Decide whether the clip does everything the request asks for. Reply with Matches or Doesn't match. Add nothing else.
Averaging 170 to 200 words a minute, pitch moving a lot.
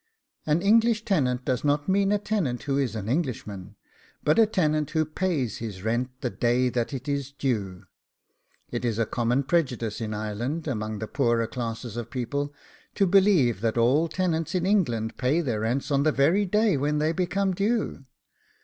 Matches